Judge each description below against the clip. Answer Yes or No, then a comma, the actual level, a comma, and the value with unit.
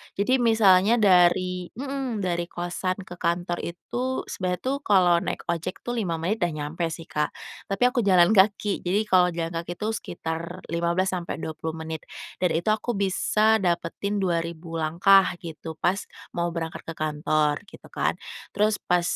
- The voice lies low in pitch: No, medium, 180 Hz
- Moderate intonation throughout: Yes, average, 3.2 semitones